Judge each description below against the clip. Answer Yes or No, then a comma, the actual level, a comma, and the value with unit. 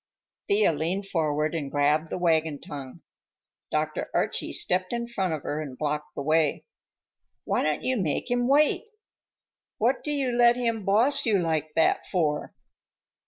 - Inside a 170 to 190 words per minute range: No, average, 160 wpm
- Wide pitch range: Yes, wide, 7.6 semitones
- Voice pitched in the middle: Yes, medium, 165 Hz